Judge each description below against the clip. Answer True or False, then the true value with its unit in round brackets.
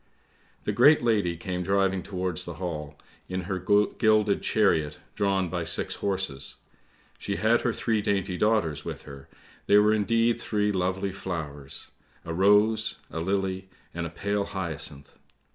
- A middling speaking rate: True (150 wpm)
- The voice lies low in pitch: True (95 Hz)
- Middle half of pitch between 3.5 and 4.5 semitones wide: False (3.1 semitones)